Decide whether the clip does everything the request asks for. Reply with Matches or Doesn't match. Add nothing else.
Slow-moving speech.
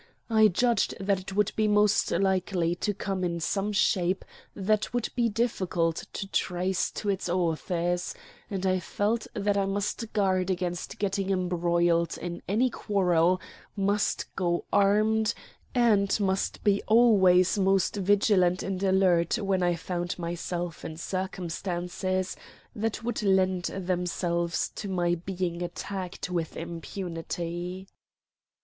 Matches